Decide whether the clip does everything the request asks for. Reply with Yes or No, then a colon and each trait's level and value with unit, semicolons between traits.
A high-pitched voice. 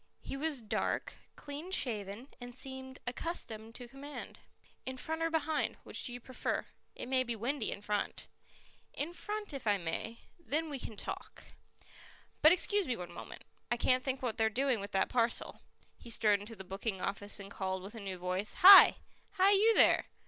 Yes: high, 245 Hz